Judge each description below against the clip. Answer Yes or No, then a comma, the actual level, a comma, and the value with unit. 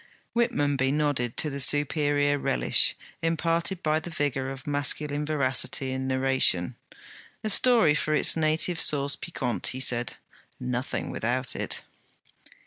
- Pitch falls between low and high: Yes, medium, 145 Hz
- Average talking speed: No, slow, 130 wpm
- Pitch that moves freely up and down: No, average, 2.7 semitones